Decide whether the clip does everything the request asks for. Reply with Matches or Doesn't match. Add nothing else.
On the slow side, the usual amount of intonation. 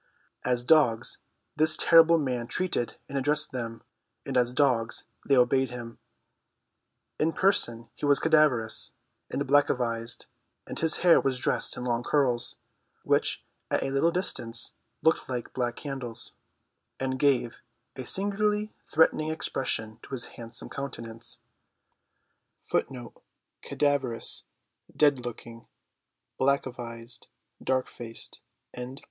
Matches